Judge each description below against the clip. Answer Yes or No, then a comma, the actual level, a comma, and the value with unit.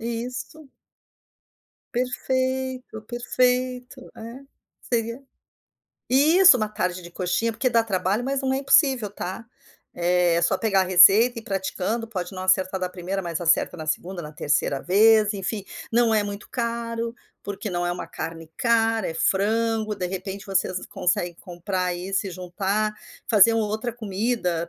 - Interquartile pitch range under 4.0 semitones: No, average, 4.3 semitones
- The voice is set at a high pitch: Yes, high, 210 Hz